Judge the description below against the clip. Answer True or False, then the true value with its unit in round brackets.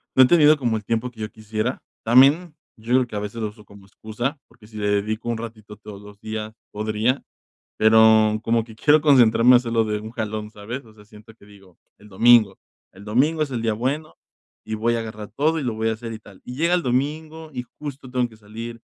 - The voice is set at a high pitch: False (115 Hz)